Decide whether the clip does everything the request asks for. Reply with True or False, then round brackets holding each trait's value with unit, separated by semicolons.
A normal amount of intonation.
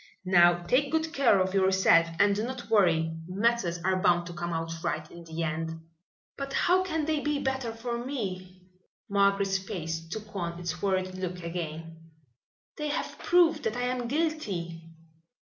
False (6.4 semitones)